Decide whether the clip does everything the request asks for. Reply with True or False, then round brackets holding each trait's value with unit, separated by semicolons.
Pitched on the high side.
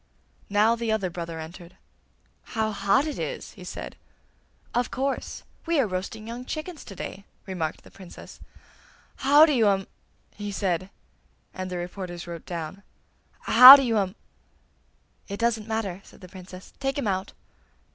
True (200 Hz)